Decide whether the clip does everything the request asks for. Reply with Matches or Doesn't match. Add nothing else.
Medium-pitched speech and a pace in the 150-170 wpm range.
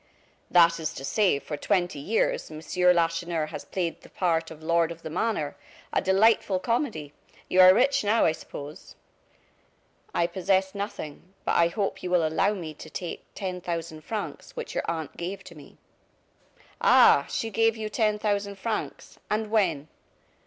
Matches